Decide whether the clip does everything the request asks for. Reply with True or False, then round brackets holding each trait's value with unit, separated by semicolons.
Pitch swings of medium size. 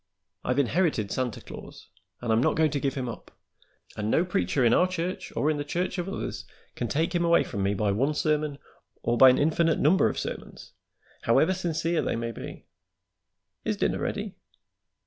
False (6.0 semitones)